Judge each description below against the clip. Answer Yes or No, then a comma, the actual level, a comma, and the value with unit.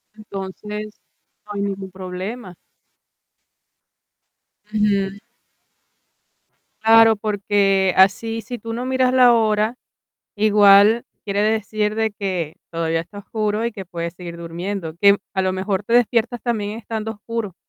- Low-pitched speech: No, high, 205 Hz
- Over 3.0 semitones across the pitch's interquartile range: No, narrow, 2.6 semitones